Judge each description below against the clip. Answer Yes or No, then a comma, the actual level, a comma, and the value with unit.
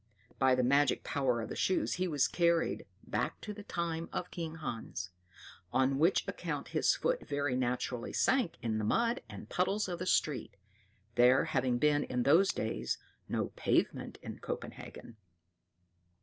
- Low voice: No, medium, 145 Hz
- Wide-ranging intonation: Yes, wide, 5.9 semitones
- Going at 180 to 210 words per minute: No, average, 160 wpm